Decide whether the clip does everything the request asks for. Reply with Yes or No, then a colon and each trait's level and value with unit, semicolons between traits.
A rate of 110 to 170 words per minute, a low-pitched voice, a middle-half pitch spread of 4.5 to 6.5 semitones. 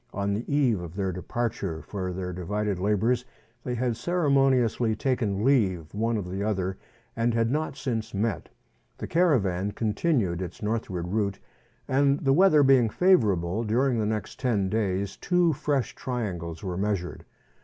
Yes: average, 155 wpm; low, 110 Hz; average, 5.1 semitones